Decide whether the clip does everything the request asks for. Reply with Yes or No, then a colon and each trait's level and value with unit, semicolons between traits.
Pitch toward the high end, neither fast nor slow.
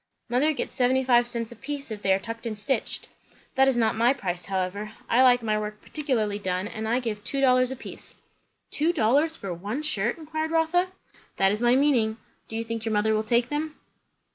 No: high, 235 Hz; fast, 215 wpm